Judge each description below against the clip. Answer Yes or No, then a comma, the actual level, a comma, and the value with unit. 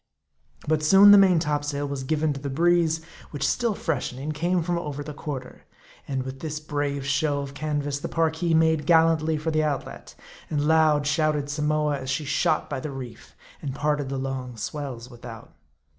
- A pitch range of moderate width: No, narrow, 2.3 semitones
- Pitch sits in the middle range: Yes, medium, 150 Hz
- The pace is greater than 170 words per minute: Yes, average, 180 wpm